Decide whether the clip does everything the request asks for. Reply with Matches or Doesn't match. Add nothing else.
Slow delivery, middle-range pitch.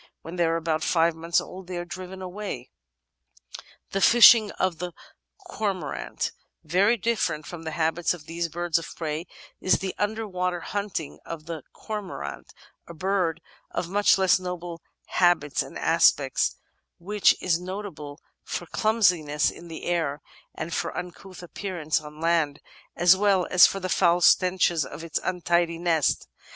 Doesn't match